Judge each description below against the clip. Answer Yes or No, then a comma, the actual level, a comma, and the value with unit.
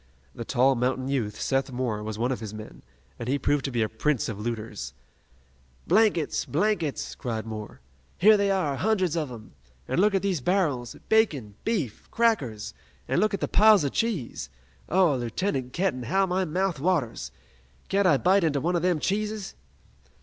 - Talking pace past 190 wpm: No, average, 180 wpm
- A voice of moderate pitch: Yes, medium, 145 Hz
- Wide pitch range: Yes, wide, 8.1 semitones